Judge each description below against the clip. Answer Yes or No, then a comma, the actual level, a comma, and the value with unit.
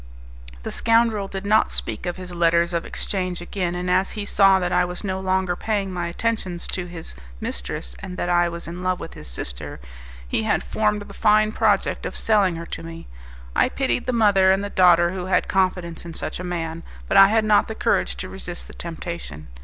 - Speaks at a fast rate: Yes, fast, 215 wpm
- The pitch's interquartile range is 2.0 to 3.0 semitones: Yes, average, 2.7 semitones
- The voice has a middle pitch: Yes, medium, 180 Hz